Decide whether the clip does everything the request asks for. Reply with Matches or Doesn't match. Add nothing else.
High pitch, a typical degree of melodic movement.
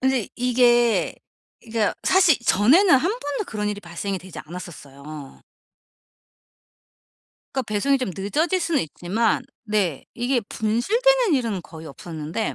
Doesn't match